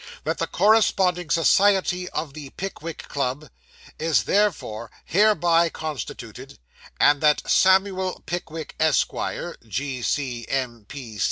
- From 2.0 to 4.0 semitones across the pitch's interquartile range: No, average, 5.1 semitones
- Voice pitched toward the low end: No, medium, 160 Hz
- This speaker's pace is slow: Yes, slow, 95 wpm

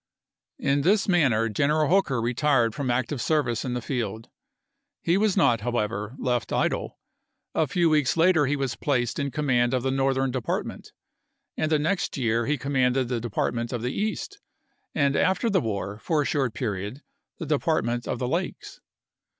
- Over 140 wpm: Yes, average, 180 wpm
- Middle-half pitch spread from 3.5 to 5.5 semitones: Yes, average, 4.2 semitones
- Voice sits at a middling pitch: No, low, 130 Hz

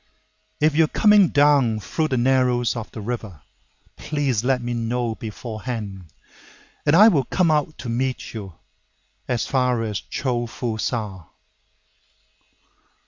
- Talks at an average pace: No, slow, 130 wpm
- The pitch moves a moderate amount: Yes, average, 4.1 semitones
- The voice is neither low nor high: No, low, 120 Hz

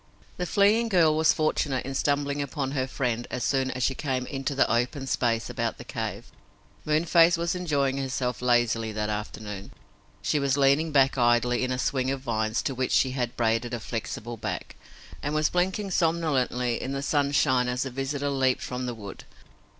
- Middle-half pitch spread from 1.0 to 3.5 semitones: Yes, average, 2.9 semitones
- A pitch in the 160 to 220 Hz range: No, low, 135 Hz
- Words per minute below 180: No, average, 185 wpm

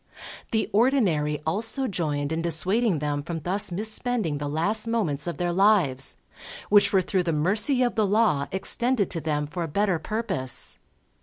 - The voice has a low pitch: No, medium, 185 Hz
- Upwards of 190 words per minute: No, average, 165 wpm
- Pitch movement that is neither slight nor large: No, wide, 5.9 semitones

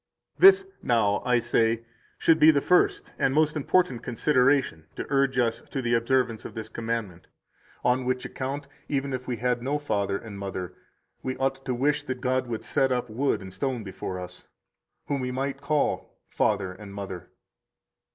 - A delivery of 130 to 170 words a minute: No, average, 180 wpm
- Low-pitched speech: Yes, low, 125 Hz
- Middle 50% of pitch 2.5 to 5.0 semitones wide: Yes, average, 3.7 semitones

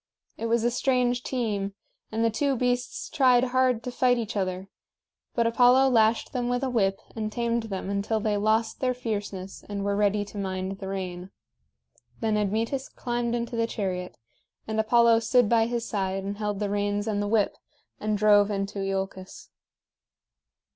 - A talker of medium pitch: No, high, 220 Hz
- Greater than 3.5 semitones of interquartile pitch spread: No, average, 3.1 semitones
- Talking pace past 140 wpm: Yes, average, 175 wpm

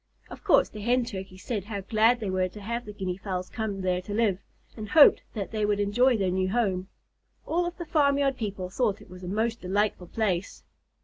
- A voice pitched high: Yes, high, 205 Hz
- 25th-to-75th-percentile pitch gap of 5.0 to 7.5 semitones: No, average, 3.8 semitones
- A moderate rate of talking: No, fast, 210 wpm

